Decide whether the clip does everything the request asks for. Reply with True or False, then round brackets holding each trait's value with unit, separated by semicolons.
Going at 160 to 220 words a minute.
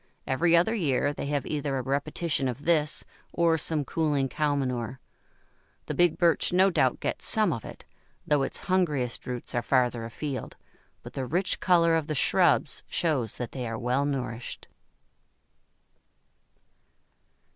False (150 wpm)